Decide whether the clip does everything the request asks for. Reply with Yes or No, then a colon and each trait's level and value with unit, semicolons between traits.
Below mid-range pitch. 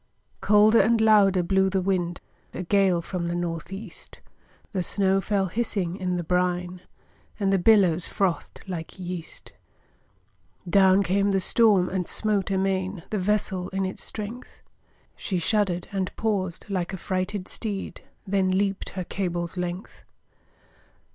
No: high, 190 Hz